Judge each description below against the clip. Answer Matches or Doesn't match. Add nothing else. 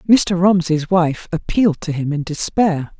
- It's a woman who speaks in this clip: Matches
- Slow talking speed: Doesn't match